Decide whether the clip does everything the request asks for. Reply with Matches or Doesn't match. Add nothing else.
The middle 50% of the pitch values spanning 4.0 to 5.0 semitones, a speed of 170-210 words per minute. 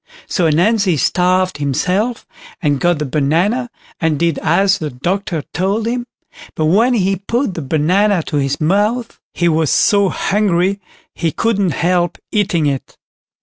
Doesn't match